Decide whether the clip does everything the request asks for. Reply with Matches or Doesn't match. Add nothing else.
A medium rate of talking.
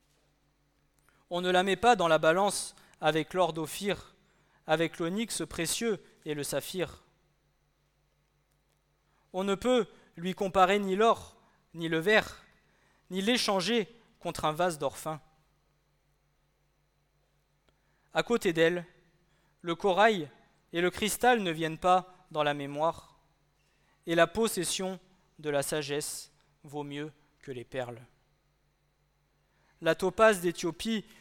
Doesn't match